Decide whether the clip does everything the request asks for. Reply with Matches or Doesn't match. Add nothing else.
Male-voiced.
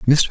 Matches